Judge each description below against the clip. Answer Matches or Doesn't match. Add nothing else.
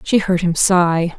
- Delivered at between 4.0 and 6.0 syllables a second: Doesn't match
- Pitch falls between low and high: Matches